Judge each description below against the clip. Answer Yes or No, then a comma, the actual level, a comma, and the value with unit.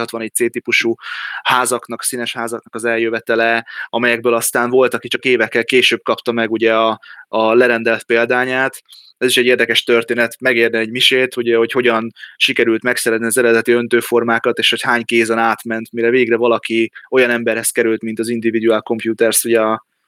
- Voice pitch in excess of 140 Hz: No, low, 115 Hz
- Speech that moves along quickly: Yes, fast, 160 wpm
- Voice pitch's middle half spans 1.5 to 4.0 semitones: No, narrow, 1.0 semitones